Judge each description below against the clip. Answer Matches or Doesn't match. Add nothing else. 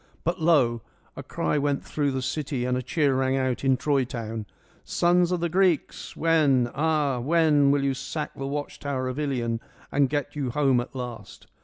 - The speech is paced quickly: Matches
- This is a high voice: Doesn't match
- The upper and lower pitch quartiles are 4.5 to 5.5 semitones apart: Doesn't match